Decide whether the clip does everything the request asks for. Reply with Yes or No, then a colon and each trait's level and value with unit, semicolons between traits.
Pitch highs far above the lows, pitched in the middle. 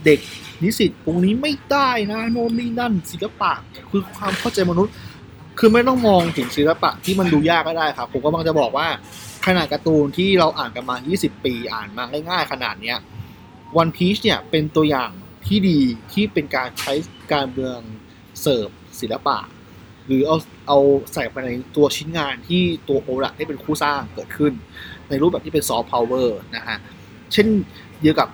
Yes: wide, 6.0 semitones; medium, 155 Hz